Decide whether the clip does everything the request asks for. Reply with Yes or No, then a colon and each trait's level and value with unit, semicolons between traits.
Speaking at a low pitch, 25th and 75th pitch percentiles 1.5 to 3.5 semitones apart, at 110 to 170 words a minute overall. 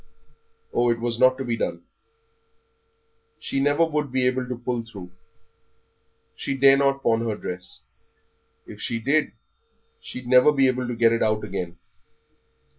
Yes: low, 125 Hz; average, 2.9 semitones; average, 155 wpm